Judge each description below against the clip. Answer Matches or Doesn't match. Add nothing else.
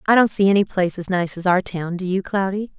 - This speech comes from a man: Doesn't match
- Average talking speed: Doesn't match